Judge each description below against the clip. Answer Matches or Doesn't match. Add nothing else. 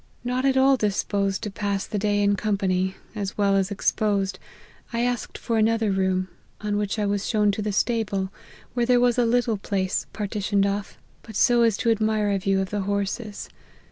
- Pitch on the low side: Doesn't match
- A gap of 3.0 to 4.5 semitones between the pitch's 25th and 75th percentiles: Doesn't match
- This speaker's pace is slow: Doesn't match